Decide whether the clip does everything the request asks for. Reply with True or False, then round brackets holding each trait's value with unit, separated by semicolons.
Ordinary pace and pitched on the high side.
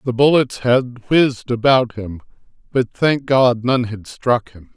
False (165 wpm; 120 Hz)